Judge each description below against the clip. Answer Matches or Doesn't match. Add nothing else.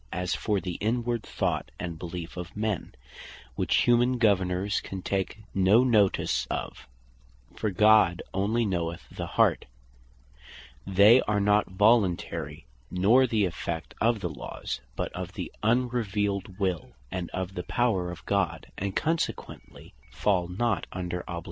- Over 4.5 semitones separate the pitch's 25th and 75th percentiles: Doesn't match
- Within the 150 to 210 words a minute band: Doesn't match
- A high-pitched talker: Doesn't match